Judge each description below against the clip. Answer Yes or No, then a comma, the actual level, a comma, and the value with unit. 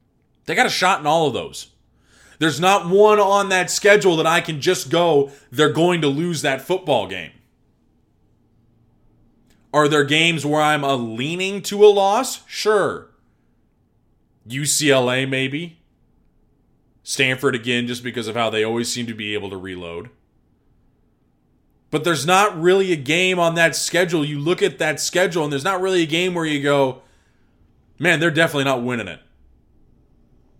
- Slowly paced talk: No, average, 160 wpm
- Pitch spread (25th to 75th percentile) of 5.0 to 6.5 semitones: Yes, wide, 5.4 semitones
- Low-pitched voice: No, medium, 150 Hz